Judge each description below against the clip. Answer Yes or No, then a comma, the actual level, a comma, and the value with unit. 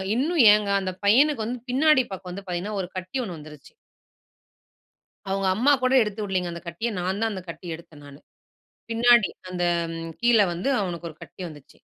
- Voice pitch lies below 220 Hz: Yes, high, 195 Hz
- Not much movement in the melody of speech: No, average, 5.1 semitones